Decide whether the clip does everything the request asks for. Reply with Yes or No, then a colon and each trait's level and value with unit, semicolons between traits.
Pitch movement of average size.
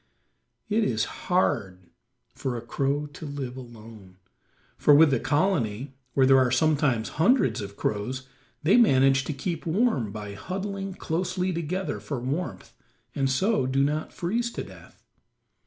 No: wide, 6.5 semitones